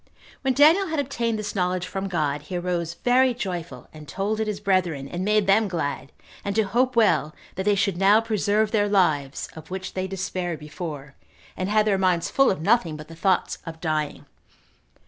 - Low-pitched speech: No, high, 190 Hz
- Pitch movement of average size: Yes, average, 4.2 semitones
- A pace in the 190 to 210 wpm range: Yes, average, 195 wpm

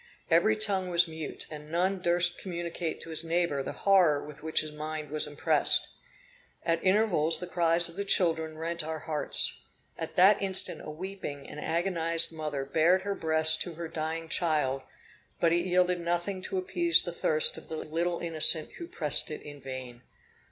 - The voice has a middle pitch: Yes, medium, 165 Hz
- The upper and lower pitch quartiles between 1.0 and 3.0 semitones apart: Yes, narrow, 2.6 semitones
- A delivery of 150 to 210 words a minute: Yes, average, 180 wpm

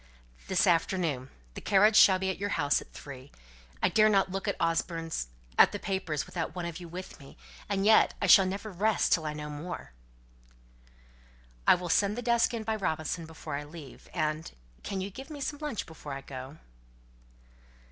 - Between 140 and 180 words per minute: No, average, 190 wpm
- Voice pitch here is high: No, medium, 180 Hz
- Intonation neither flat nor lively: Yes, average, 4.6 semitones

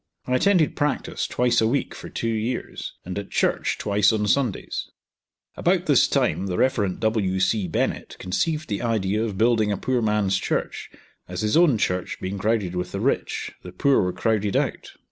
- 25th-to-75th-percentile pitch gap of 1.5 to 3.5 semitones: No, average, 3.9 semitones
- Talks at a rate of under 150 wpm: No, average, 185 wpm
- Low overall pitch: Yes, low, 105 Hz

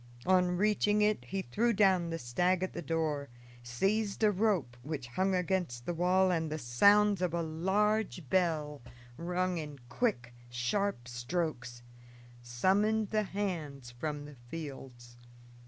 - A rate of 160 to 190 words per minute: No, average, 140 wpm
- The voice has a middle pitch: Yes, medium, 170 Hz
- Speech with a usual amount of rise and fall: No, wide, 5.9 semitones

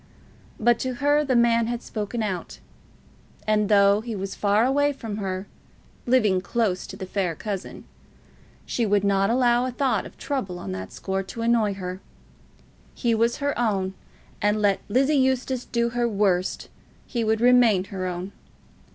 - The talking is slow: No, average, 165 wpm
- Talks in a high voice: Yes, high, 215 Hz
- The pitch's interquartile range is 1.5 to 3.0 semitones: No, average, 3.7 semitones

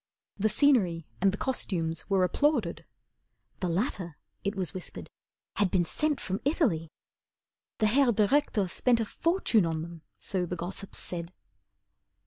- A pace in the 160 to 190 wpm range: No, average, 140 wpm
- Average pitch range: No, wide, 5.8 semitones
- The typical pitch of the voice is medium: No, high, 195 Hz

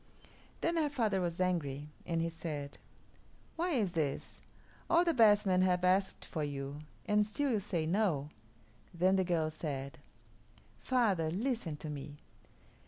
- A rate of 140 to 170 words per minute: Yes, average, 150 wpm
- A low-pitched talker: No, medium, 180 Hz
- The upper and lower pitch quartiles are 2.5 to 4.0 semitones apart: No, average, 5.2 semitones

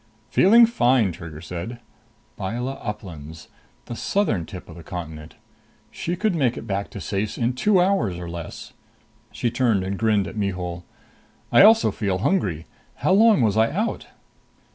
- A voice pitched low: Yes, low, 105 Hz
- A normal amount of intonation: No, wide, 7.2 semitones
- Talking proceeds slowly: No, average, 160 wpm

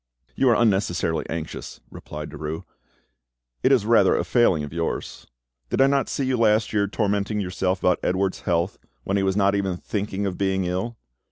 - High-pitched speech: No, very low, 95 Hz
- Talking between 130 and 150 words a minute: No, average, 180 wpm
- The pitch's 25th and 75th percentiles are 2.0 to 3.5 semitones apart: Yes, average, 2.9 semitones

